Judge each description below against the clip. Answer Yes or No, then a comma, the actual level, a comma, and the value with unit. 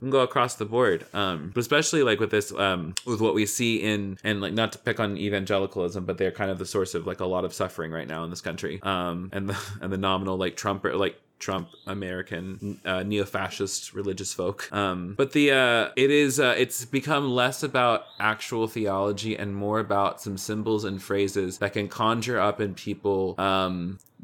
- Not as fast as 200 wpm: No, fast, 205 wpm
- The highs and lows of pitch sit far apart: No, average, 3.1 semitones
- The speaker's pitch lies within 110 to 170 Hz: No, low, 100 Hz